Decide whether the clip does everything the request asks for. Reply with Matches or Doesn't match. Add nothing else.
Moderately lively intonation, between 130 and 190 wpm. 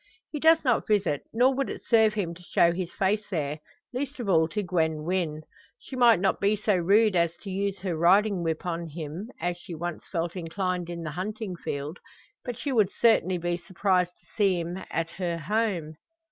Doesn't match